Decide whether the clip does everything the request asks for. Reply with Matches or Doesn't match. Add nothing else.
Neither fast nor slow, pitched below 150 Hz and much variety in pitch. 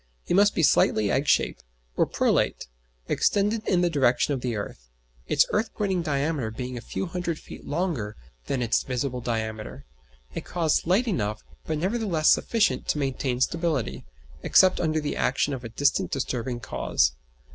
Matches